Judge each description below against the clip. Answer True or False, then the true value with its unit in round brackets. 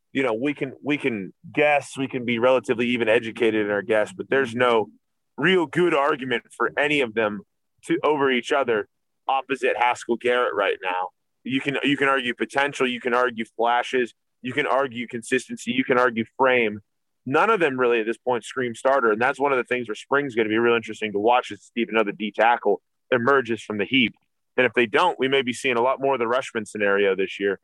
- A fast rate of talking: True (225 wpm)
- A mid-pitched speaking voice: False (125 Hz)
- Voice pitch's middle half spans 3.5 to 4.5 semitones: False (3.1 semitones)